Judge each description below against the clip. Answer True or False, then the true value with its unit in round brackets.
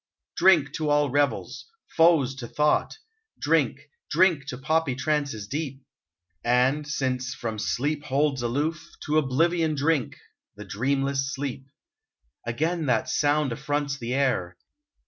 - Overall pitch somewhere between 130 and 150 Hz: True (140 Hz)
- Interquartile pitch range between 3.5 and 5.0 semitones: False (2.9 semitones)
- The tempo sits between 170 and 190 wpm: False (135 wpm)